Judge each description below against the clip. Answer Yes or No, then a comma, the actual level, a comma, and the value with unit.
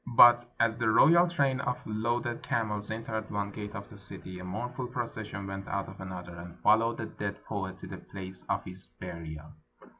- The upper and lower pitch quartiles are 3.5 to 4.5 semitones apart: Yes, average, 3.9 semitones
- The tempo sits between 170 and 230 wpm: Yes, average, 190 wpm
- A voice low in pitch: Yes, low, 105 Hz